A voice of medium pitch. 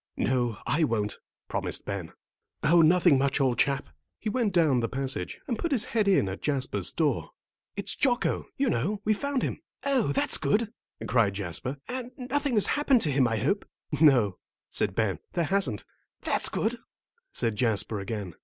Yes: medium, 145 Hz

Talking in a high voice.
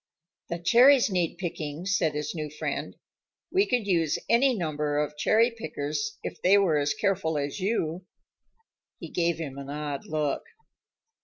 No: medium, 165 Hz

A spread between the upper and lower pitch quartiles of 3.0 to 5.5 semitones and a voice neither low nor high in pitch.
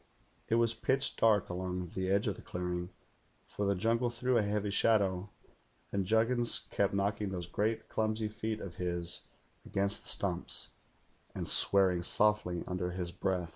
No: average, 3.3 semitones; low, 100 Hz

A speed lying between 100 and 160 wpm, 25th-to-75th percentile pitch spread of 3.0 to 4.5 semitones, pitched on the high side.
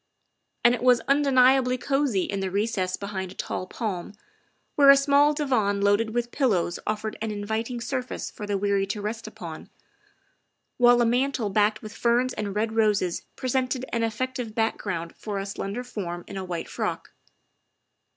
No: average, 175 wpm; average, 3.9 semitones; high, 220 Hz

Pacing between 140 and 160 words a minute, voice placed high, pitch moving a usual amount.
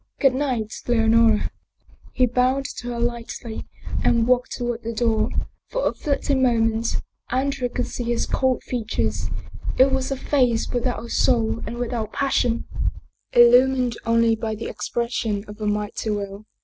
No: average, 155 wpm; high, 235 Hz; narrow, 2.2 semitones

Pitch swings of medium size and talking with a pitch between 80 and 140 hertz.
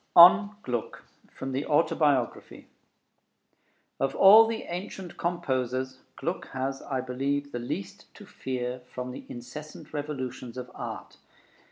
Yes: average, 3.4 semitones; low, 135 Hz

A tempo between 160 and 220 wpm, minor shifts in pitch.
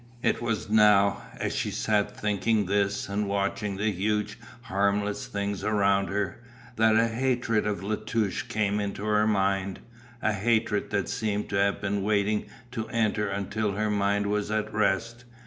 Yes: average, 165 wpm; narrow, 1.4 semitones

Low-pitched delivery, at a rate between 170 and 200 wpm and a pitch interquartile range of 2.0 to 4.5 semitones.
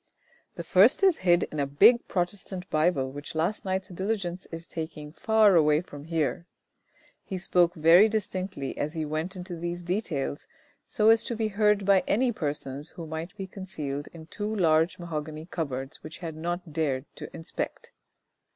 No: medium, 170 Hz; average, 175 wpm; average, 3.7 semitones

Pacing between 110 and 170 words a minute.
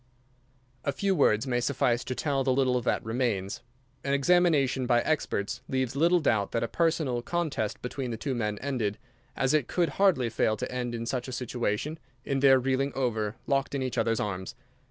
No: average, 190 wpm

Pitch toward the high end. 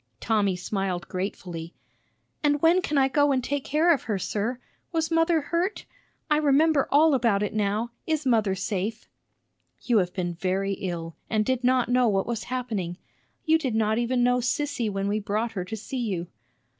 Yes: high, 230 Hz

